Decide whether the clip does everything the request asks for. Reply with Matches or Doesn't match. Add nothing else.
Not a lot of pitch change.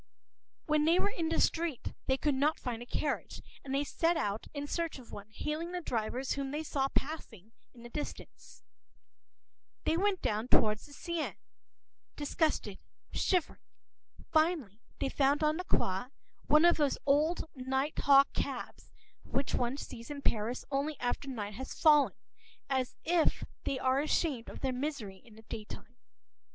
Doesn't match